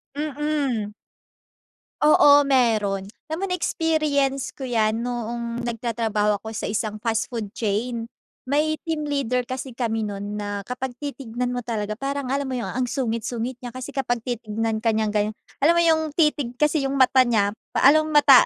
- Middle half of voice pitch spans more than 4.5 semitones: No, average, 4.2 semitones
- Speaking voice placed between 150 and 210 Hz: No, high, 245 Hz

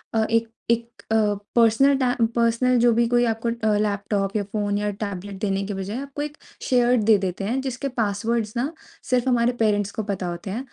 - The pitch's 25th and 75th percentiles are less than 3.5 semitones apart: Yes, average, 3.1 semitones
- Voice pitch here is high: Yes, high, 225 Hz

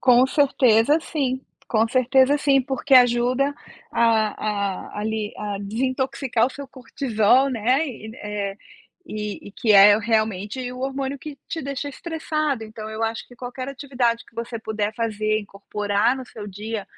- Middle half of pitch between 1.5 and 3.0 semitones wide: No, average, 3.8 semitones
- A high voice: Yes, high, 235 Hz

